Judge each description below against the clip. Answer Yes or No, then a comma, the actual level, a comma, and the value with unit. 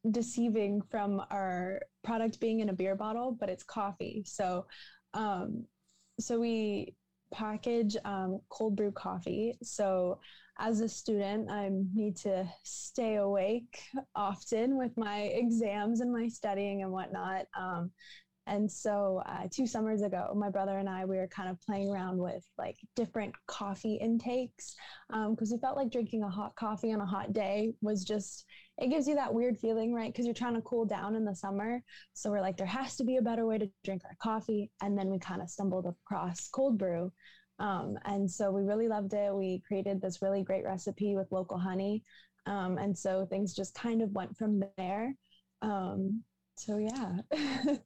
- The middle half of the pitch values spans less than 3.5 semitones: Yes, average, 2.7 semitones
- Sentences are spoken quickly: No, average, 180 wpm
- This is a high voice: Yes, high, 205 Hz